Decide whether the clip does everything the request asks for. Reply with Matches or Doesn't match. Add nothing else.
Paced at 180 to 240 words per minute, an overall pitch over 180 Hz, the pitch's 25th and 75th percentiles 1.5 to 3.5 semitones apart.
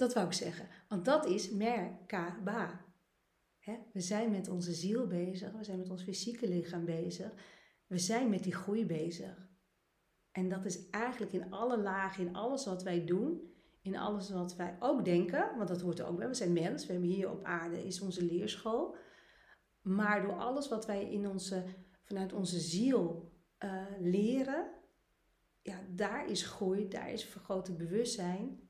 Doesn't match